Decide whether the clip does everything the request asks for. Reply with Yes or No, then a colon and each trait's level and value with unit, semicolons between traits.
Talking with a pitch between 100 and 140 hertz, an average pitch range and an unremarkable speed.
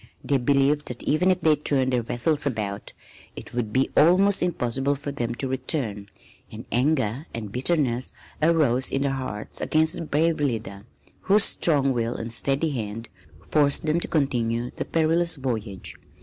Yes: low, 135 Hz; average, 4.6 semitones; average, 165 wpm